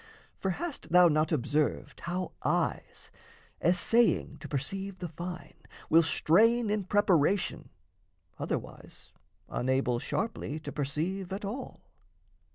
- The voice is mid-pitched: Yes, medium, 180 Hz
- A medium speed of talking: No, slow, 110 wpm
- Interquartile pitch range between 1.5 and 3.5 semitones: No, average, 4.6 semitones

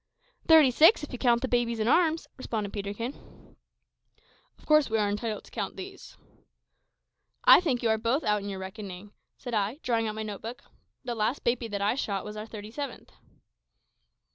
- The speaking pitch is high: Yes, high, 230 Hz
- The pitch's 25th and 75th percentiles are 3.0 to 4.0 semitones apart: Yes, average, 3.6 semitones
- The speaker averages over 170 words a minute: Yes, average, 190 wpm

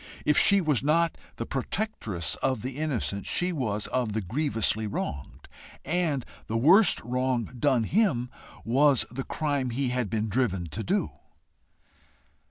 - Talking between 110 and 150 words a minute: Yes, average, 145 wpm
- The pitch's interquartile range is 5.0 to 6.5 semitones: Yes, average, 5.3 semitones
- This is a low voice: Yes, low, 130 Hz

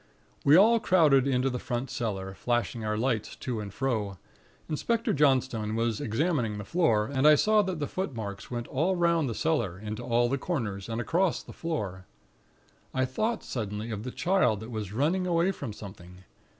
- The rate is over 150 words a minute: Yes, average, 180 wpm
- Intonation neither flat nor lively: No, wide, 6.9 semitones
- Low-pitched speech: Yes, low, 125 Hz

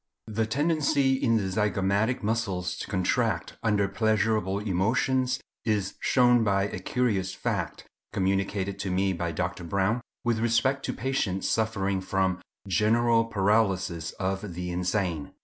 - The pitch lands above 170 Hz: No, low, 100 Hz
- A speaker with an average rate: No, slow, 130 wpm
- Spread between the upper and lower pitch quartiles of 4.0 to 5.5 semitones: No, average, 3.3 semitones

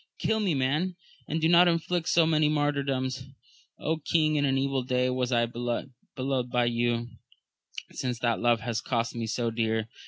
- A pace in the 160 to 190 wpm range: Yes, average, 165 wpm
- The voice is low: Yes, low, 130 Hz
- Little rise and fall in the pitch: No, average, 4.1 semitones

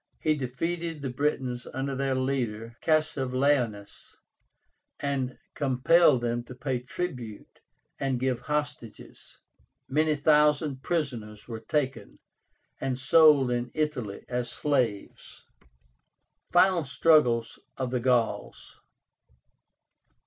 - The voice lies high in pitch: No, low, 130 Hz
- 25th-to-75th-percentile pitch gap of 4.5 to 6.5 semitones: No, average, 3.4 semitones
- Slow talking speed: Yes, slow, 100 wpm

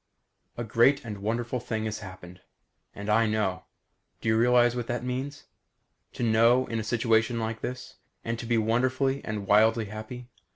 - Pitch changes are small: Yes, narrow, 2.1 semitones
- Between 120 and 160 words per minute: No, average, 170 wpm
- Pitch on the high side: No, low, 115 Hz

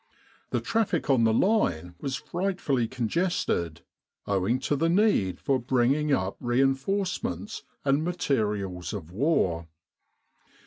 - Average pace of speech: No, slow, 120 wpm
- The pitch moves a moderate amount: No, wide, 8.8 semitones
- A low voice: Yes, low, 130 Hz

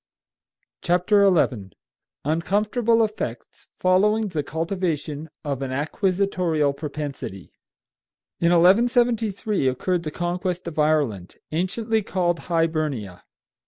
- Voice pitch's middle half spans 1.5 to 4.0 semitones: No, average, 4.9 semitones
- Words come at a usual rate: No, slow, 95 wpm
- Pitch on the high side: No, medium, 170 Hz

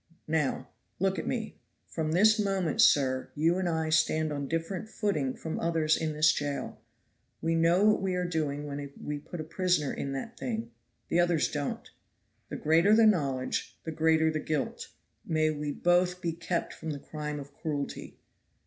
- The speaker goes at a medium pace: Yes, average, 180 wpm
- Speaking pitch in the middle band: Yes, medium, 160 Hz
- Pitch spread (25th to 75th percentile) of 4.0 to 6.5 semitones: No, average, 3.2 semitones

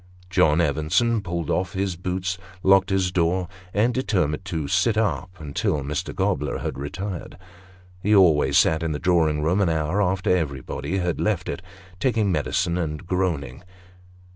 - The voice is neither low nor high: No, very low, 90 Hz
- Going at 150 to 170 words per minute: Yes, average, 160 wpm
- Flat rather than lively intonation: No, average, 3.7 semitones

